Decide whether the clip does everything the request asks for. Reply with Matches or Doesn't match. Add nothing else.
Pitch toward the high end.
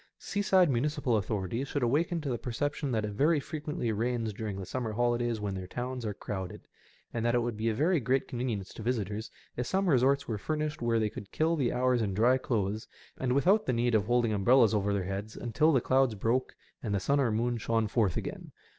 Doesn't match